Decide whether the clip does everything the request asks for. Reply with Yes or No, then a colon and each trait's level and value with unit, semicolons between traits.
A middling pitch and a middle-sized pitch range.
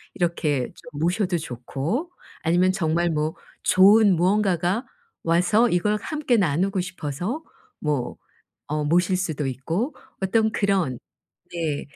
Yes: medium, 175 Hz; average, 4.4 semitones